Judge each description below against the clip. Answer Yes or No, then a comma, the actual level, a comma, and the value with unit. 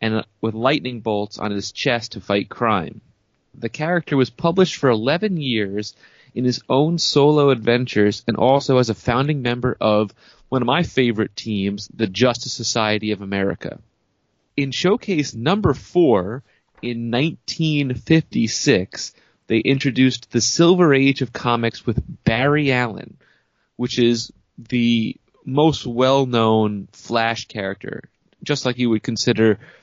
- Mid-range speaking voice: No, low, 120 Hz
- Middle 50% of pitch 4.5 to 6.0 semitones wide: No, average, 3.8 semitones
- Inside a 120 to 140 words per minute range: Yes, slow, 135 wpm